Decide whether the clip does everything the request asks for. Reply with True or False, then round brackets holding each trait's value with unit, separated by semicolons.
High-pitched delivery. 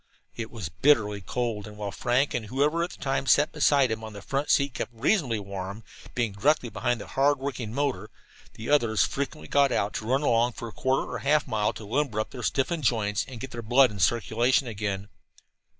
False (120 Hz)